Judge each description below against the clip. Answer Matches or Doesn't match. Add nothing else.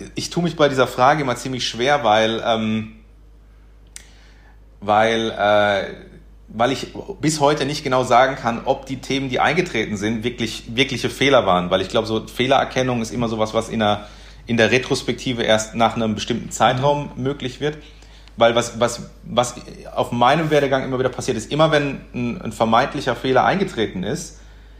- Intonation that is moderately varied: Matches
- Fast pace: Doesn't match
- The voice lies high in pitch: Doesn't match